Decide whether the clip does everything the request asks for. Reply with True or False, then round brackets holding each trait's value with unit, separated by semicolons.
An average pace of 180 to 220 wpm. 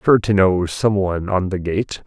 True (205 wpm)